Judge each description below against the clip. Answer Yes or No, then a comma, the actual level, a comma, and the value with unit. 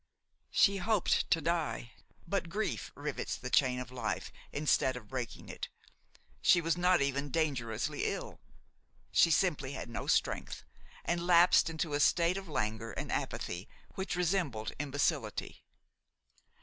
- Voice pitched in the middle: Yes, medium, 150 Hz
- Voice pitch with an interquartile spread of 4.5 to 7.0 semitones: Yes, average, 5.3 semitones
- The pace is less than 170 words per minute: Yes, slow, 135 wpm